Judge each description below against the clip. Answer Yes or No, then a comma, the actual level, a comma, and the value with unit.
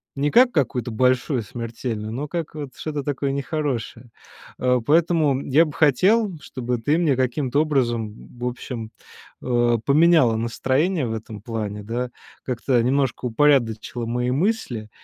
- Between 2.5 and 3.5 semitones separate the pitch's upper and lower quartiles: No, average, 4.0 semitones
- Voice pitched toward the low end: Yes, low, 130 Hz